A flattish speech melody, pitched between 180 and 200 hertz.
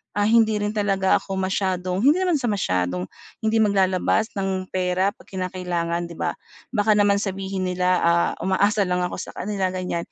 Yes: narrow, 2.2 semitones; high, 190 Hz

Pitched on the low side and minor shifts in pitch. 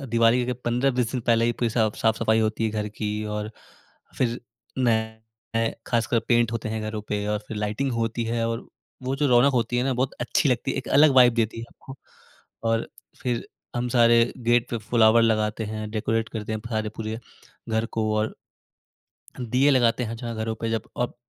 Yes: low, 115 Hz; narrow, 1.6 semitones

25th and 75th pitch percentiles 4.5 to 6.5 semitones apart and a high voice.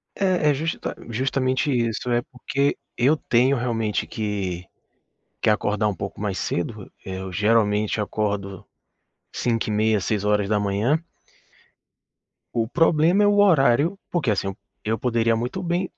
No: average, 4.9 semitones; low, 115 Hz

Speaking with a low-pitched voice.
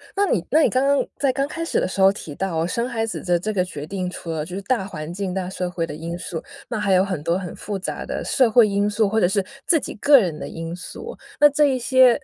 No: high, 195 Hz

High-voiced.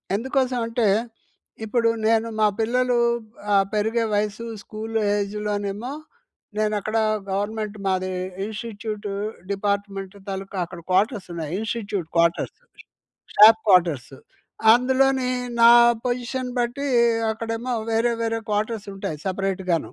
Yes: high, 215 Hz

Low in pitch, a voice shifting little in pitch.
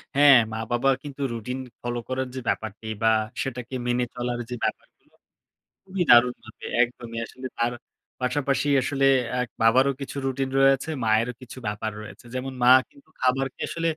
Yes: low, 125 Hz; narrow, 2.2 semitones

